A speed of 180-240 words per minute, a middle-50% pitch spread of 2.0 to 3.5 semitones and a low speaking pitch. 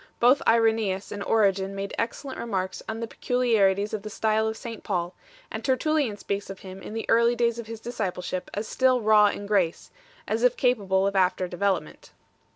No: average, 200 wpm; average, 3.1 semitones; high, 215 Hz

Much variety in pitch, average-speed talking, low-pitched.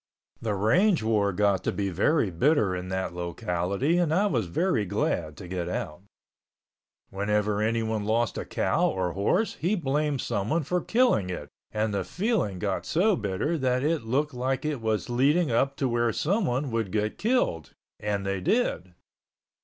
Yes: wide, 7.5 semitones; average, 170 wpm; low, 110 Hz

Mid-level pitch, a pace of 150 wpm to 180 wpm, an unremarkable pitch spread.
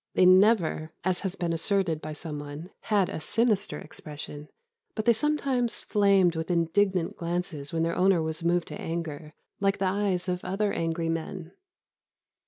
Yes: medium, 175 Hz; average, 165 wpm; average, 3.4 semitones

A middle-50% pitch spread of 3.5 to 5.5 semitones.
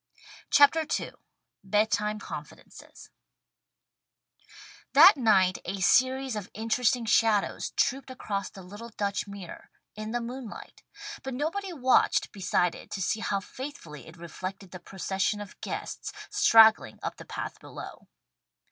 Yes: average, 4.5 semitones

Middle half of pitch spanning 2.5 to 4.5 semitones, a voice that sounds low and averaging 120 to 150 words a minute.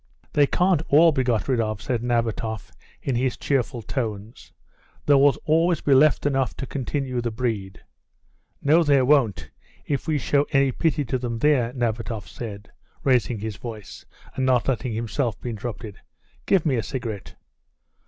No: average, 3.8 semitones; low, 125 Hz; average, 165 wpm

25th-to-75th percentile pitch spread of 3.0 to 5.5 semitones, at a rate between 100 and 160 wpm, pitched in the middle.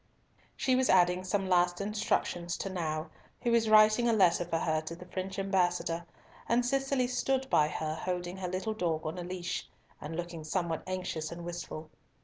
No: average, 3.8 semitones; average, 180 wpm; medium, 180 Hz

